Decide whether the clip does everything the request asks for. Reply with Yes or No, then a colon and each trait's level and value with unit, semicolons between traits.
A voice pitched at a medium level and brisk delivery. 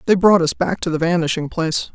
Yes: medium, 170 Hz; fast, 245 wpm